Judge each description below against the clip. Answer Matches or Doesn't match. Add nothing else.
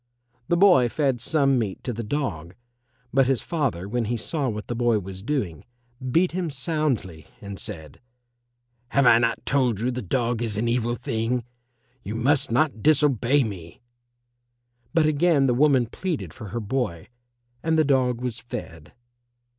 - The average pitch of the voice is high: Doesn't match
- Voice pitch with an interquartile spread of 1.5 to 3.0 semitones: Doesn't match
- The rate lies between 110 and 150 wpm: Doesn't match